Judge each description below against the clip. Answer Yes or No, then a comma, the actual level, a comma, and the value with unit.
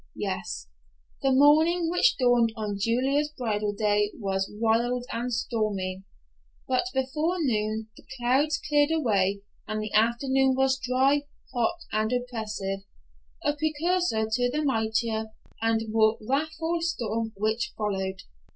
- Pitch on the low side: No, high, 235 Hz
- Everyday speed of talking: No, slow, 125 wpm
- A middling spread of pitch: Yes, average, 4.7 semitones